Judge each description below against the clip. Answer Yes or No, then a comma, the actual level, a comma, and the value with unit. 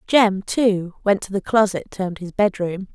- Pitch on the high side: Yes, high, 195 Hz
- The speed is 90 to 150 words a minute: No, fast, 205 wpm